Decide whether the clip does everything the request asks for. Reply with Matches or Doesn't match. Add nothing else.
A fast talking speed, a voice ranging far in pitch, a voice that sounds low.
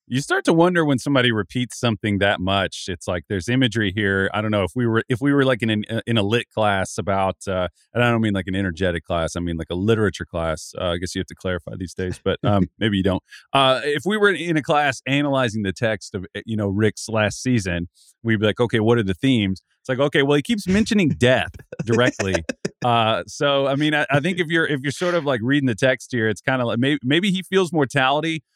Matches